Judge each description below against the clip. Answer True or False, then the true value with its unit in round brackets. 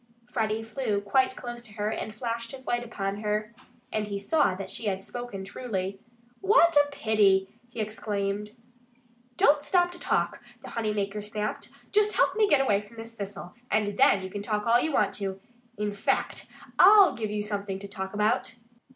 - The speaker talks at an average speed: True (190 wpm)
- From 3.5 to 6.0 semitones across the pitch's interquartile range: False (3.0 semitones)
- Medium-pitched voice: False (215 Hz)